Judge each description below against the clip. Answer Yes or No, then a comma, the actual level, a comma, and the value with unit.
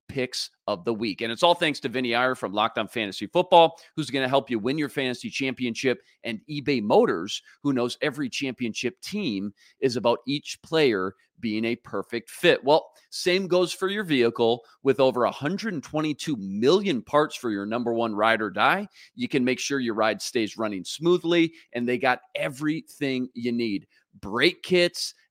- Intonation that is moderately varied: No, wide, 6.0 semitones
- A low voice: Yes, low, 130 Hz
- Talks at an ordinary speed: Yes, average, 180 wpm